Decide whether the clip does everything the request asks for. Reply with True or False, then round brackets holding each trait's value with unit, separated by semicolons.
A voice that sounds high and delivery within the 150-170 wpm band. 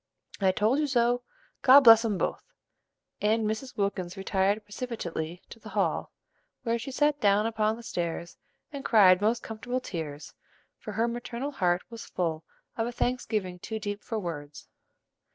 True (215 Hz; 160 wpm)